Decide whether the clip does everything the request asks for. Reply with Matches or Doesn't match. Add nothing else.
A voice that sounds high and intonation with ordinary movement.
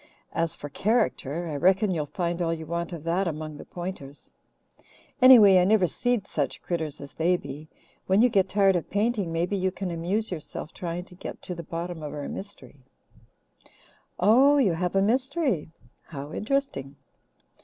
Doesn't match